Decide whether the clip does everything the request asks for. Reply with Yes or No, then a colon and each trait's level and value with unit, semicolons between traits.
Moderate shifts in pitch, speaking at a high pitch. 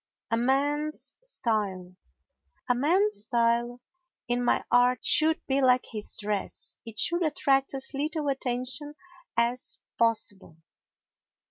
Yes: average, 3.8 semitones; very high, 250 Hz